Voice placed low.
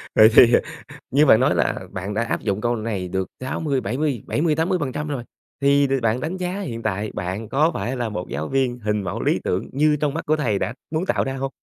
Yes: low, 125 Hz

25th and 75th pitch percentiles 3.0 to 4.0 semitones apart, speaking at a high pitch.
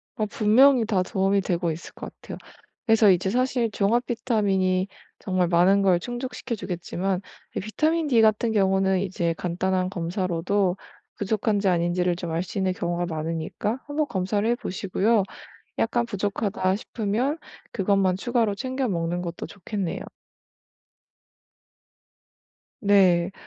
Yes: average, 3.6 semitones; high, 195 Hz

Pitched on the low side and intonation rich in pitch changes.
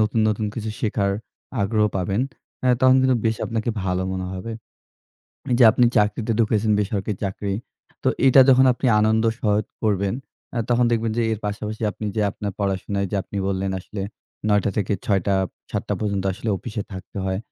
No: low, 105 Hz; narrow, 2.4 semitones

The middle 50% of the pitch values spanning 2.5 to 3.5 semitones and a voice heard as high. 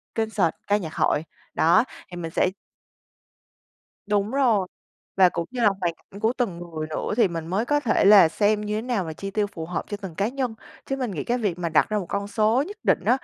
No: average, 4.3 semitones; high, 205 Hz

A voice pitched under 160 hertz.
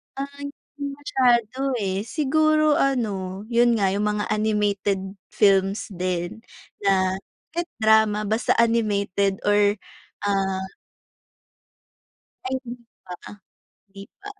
No: high, 210 Hz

